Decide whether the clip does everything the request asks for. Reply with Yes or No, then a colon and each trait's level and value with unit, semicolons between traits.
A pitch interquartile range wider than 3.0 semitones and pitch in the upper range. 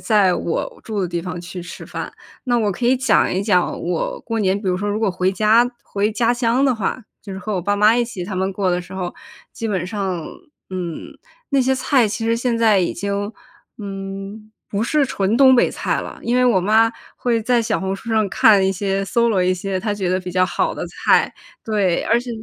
Yes: average, 3.5 semitones; high, 205 Hz